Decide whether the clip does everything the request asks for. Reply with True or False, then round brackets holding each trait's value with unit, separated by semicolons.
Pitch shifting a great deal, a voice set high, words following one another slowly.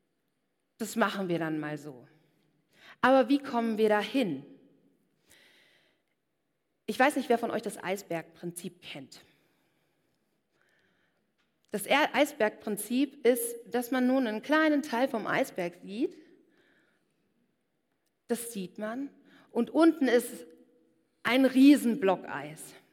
True (5.8 semitones; 235 Hz; 110 wpm)